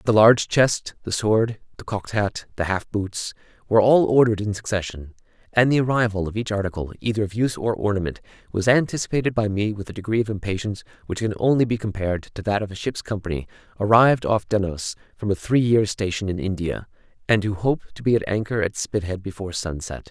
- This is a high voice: No, low, 105 Hz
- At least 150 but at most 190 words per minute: No, fast, 205 wpm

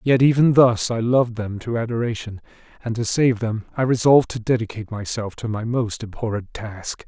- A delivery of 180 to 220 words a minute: Yes, average, 185 wpm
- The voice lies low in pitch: Yes, low, 115 Hz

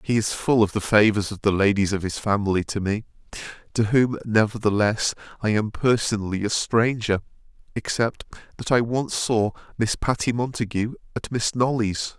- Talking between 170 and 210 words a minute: No, average, 160 wpm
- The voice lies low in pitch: Yes, low, 110 Hz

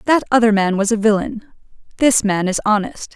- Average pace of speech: Yes, average, 190 wpm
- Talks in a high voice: Yes, high, 220 Hz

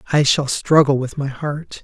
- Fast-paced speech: No, average, 195 wpm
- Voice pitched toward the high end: No, medium, 140 Hz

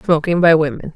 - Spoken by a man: No, female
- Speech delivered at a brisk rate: No, average, 190 wpm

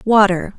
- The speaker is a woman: Yes, female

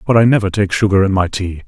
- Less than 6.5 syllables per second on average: No, 6.6 syllables/s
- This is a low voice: Yes, low, 100 Hz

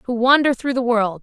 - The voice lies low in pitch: No, high, 245 Hz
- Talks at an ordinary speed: No, fast, 245 wpm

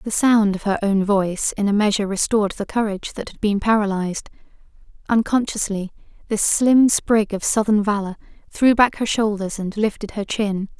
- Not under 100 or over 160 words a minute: No, average, 170 wpm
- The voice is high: Yes, high, 210 Hz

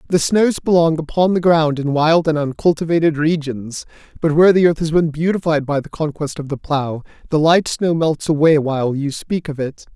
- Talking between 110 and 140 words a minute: No, fast, 205 wpm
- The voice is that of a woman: No, male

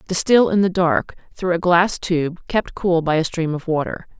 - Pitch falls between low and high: Yes, medium, 175 Hz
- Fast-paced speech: Yes, fast, 215 wpm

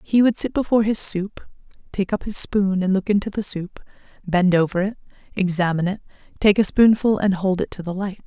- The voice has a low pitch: No, high, 195 Hz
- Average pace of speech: No, fast, 210 wpm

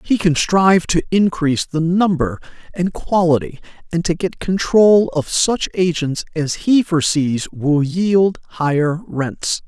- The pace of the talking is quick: No, average, 145 wpm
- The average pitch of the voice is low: No, medium, 170 Hz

